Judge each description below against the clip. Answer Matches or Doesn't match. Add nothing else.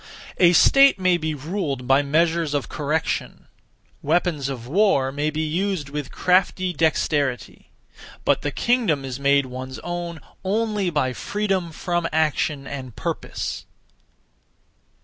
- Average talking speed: Doesn't match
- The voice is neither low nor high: Matches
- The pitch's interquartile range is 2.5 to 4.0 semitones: Doesn't match